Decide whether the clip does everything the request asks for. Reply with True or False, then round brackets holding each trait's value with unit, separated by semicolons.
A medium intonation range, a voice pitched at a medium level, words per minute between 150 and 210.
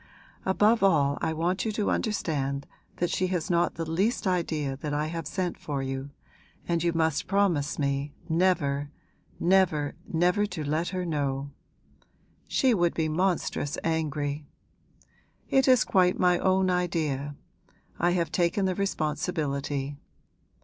False (4.0 semitones; 165 Hz; 140 wpm)